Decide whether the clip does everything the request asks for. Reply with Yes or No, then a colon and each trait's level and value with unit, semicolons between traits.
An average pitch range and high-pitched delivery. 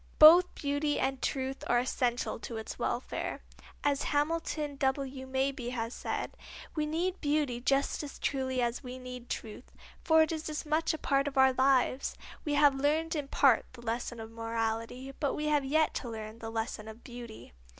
Yes: average, 3.4 semitones; very high, 265 Hz